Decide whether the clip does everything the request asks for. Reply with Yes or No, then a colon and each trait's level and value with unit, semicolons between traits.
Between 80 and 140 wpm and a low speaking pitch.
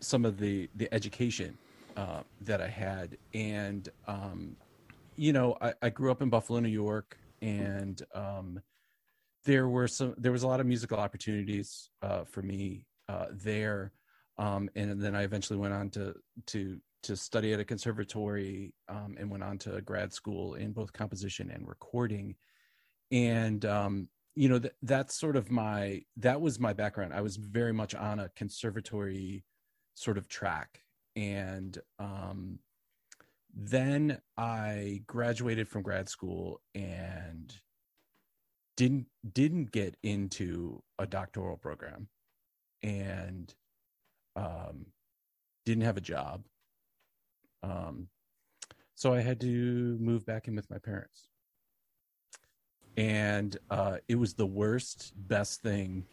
Yes: slow, 135 wpm; low, 105 Hz